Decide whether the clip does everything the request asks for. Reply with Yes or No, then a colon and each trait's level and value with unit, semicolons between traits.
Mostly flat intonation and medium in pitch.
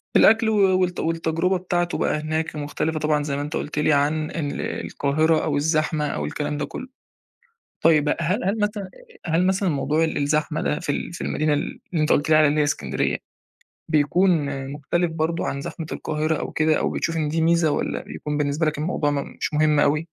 Yes: narrow, 2.1 semitones; medium, 155 Hz